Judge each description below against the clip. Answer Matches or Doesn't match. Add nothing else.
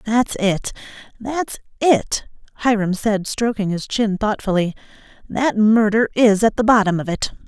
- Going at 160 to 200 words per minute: Doesn't match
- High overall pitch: Matches